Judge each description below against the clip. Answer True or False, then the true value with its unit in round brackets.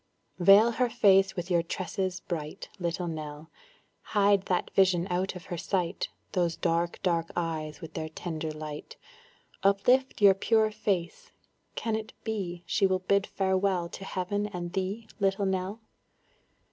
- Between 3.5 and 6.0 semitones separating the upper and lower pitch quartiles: False (2.7 semitones)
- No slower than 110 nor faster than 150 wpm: True (145 wpm)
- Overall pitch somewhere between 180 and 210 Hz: True (185 Hz)